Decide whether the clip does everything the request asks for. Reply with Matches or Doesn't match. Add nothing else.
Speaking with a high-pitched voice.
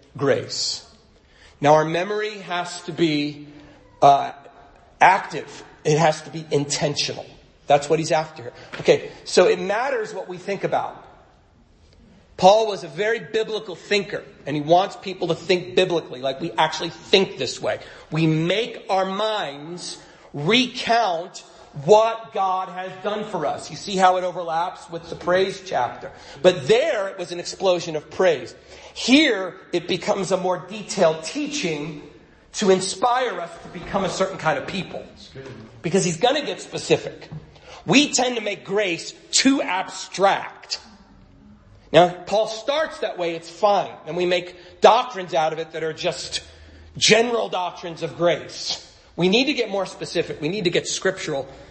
Doesn't match